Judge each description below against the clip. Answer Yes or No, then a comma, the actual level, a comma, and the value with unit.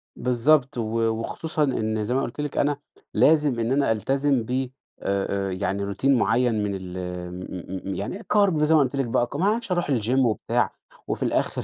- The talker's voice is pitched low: Yes, low, 120 Hz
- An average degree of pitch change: No, wide, 5.9 semitones